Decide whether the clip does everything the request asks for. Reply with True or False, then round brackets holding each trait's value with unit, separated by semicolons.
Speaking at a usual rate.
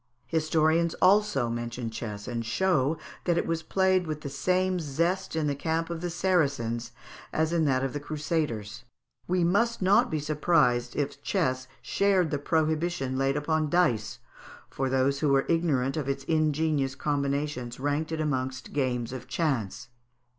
True (160 wpm)